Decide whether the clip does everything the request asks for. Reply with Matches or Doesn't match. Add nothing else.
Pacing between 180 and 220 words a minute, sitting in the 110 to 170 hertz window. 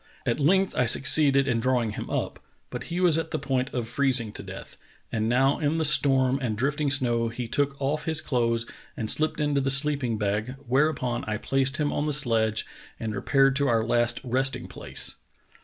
Matches